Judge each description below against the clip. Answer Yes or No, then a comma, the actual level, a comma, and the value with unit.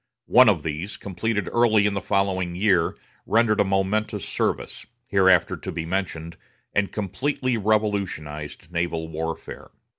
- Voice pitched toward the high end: No, very low, 95 Hz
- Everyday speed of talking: No, slow, 130 wpm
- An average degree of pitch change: Yes, average, 3.9 semitones